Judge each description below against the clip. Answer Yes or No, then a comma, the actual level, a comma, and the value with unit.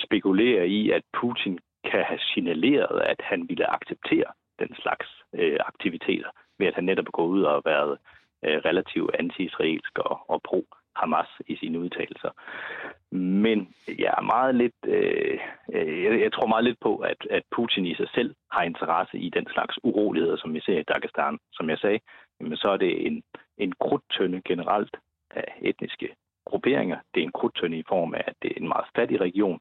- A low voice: No, very high, 370 Hz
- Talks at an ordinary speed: Yes, average, 185 wpm